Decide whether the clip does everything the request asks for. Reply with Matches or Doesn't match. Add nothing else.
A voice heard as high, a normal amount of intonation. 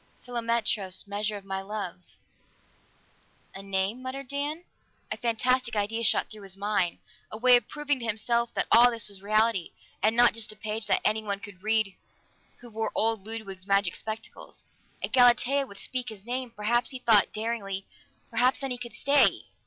Matches